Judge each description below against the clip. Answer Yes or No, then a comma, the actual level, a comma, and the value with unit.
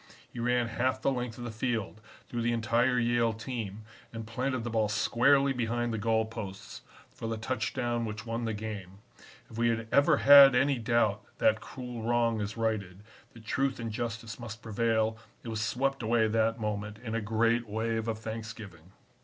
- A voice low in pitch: Yes, low, 115 Hz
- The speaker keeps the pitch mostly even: Yes, narrow, 1.6 semitones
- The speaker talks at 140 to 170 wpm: No, average, 185 wpm